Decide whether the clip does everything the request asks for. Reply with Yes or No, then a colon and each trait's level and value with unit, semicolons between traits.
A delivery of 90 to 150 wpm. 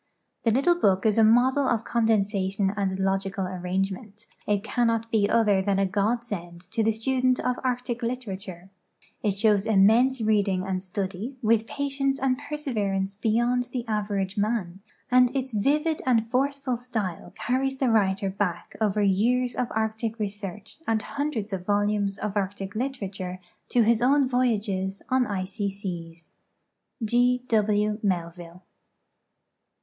Yes: average, 145 wpm